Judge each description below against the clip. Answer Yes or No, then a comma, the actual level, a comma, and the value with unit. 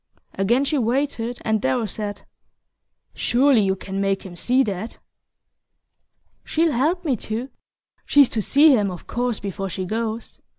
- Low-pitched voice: No, high, 230 Hz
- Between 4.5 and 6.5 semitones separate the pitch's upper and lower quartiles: Yes, average, 5.1 semitones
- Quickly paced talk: No, average, 145 wpm